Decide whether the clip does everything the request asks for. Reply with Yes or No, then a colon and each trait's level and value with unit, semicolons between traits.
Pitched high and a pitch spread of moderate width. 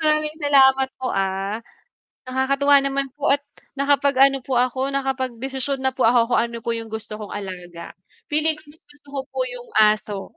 Yes: very high, 265 Hz; average, 3.7 semitones